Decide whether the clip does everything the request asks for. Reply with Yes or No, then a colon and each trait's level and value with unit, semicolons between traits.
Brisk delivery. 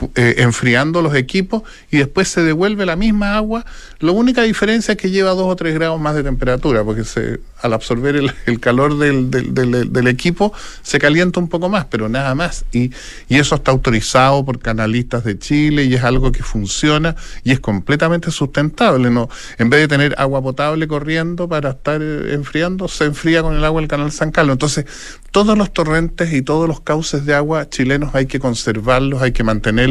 Yes: fast, 200 wpm